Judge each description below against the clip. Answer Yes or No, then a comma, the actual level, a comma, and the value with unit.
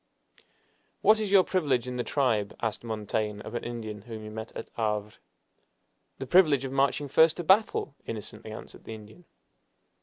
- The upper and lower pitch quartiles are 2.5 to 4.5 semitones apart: No, average, 5.3 semitones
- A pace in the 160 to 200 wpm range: Yes, average, 170 wpm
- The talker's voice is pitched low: Yes, low, 120 Hz